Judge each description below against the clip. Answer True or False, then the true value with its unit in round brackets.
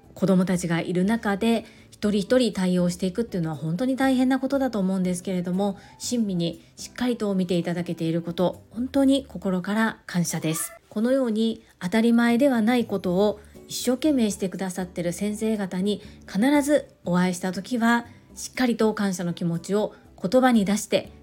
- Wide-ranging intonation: False (4.5 semitones)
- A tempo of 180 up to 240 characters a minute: False (375 characters per minute)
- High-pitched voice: True (200 Hz)